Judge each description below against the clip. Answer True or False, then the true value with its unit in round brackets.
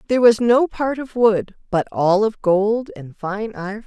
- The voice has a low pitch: False (220 Hz)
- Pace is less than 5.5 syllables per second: True (4.7 syllables/s)